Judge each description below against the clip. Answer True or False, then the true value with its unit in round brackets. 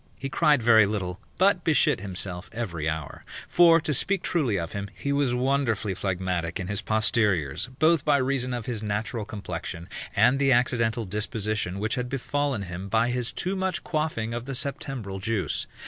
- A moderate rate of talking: True (175 wpm)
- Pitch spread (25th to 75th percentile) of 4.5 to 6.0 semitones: True (5.5 semitones)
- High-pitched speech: False (115 Hz)